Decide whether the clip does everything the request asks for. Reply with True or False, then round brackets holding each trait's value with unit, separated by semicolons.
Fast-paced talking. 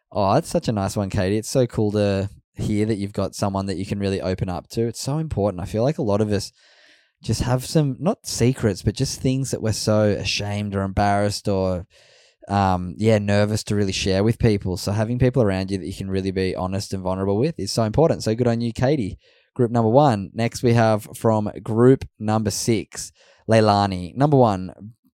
True (215 wpm)